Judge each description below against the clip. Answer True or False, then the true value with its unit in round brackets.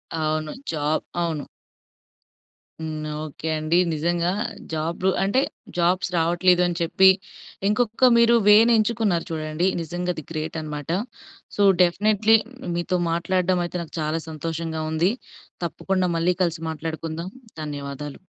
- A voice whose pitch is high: False (170 Hz)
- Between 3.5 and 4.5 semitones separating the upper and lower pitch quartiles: False (2.8 semitones)